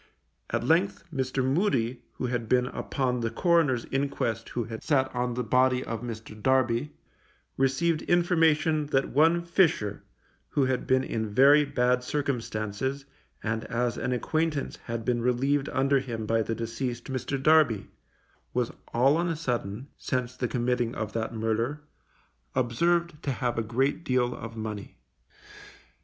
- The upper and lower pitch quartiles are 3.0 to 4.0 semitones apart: Yes, average, 3.6 semitones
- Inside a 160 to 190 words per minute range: No, average, 150 wpm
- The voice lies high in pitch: No, low, 125 Hz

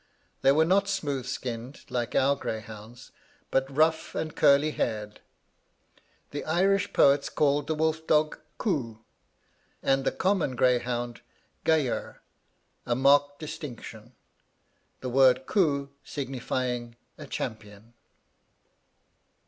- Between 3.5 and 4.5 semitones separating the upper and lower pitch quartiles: Yes, average, 4.2 semitones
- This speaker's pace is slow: Yes, slow, 110 wpm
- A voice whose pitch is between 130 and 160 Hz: Yes, low, 135 Hz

